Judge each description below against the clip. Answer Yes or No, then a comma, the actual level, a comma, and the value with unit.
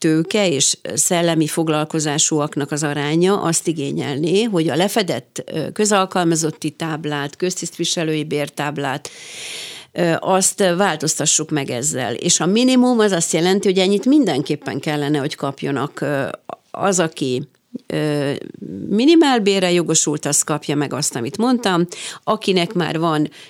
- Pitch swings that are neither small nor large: Yes, average, 4.3 semitones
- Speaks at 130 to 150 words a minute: No, average, 110 wpm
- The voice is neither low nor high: Yes, medium, 160 Hz